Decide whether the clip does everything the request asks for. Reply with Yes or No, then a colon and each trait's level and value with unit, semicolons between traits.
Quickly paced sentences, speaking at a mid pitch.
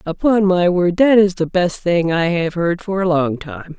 Yes: fast, 240 wpm; medium, 175 Hz